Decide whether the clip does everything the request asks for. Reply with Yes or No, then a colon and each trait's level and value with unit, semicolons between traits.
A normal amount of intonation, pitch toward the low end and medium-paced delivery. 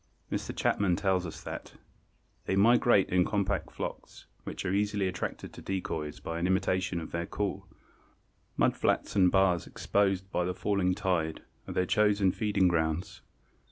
No: narrow, 2.0 semitones; very low, 95 Hz; average, 155 wpm